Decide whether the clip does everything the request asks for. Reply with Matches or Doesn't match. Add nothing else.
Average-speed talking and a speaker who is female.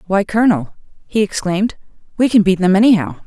Matches